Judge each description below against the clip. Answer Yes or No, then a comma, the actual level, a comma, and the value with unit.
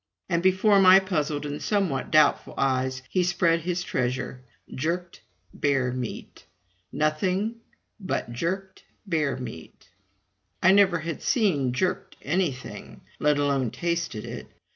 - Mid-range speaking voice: Yes, medium, 165 Hz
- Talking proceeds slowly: Yes, slow, 120 wpm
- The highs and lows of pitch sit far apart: Yes, wide, 5.8 semitones